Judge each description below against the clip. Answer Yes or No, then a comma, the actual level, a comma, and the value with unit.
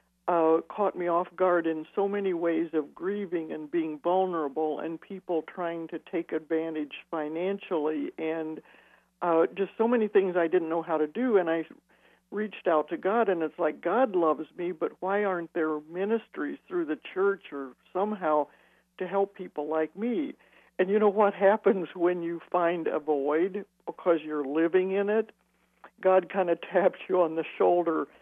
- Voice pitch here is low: No, medium, 175 Hz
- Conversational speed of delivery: Yes, average, 175 wpm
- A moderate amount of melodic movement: Yes, average, 3.4 semitones